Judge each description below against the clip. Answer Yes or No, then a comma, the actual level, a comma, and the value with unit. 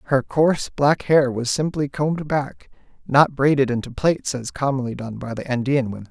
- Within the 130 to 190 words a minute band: Yes, average, 185 wpm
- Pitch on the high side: No, low, 135 Hz